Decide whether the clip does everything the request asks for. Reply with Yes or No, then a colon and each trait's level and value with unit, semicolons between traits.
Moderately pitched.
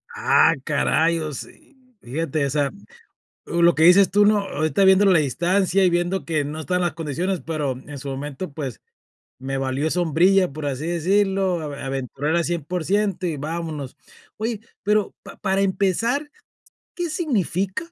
Yes: medium, 170 Hz